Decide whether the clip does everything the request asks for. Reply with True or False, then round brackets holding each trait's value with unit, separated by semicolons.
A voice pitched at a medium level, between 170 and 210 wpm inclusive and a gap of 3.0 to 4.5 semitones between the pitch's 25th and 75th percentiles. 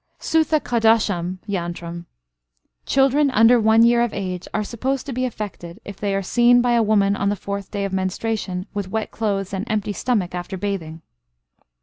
False (205 Hz; 175 wpm; 3.8 semitones)